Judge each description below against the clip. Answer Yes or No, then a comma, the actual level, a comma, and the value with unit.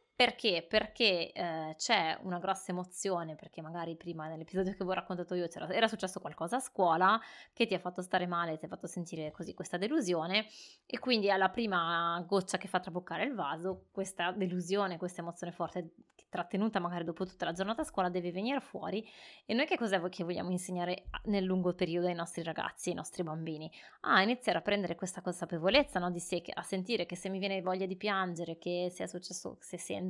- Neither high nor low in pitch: Yes, medium, 180 Hz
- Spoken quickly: Yes, fast, 205 wpm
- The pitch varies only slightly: Yes, narrow, 2.2 semitones